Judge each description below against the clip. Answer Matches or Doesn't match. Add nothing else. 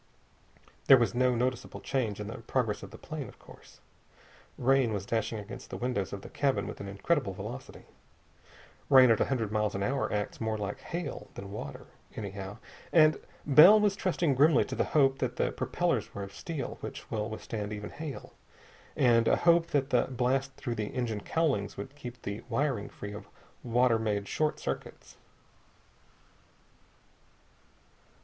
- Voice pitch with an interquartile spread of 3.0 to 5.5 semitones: Matches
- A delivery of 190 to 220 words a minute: Doesn't match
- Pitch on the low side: Matches